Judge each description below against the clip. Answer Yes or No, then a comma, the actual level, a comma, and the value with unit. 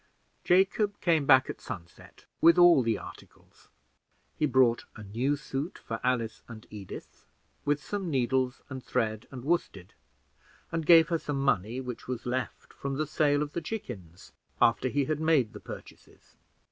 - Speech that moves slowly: No, average, 160 wpm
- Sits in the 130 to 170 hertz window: Yes, low, 135 Hz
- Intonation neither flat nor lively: Yes, average, 4.8 semitones